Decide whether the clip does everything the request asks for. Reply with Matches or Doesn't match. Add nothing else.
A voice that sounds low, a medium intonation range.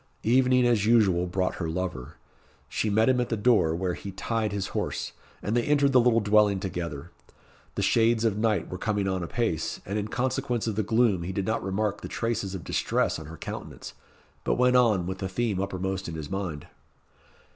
Matches